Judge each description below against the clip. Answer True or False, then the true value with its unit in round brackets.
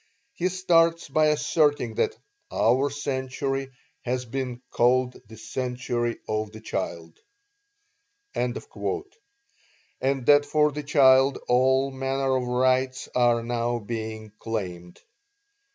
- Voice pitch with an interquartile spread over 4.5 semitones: False (3.1 semitones)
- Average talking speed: False (105 wpm)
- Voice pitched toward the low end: True (130 Hz)